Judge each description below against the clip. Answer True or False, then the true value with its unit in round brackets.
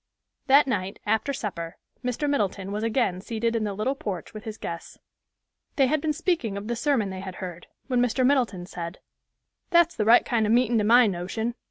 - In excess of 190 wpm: True (200 wpm)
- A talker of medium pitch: False (225 Hz)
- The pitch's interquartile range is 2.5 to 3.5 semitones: False (4.5 semitones)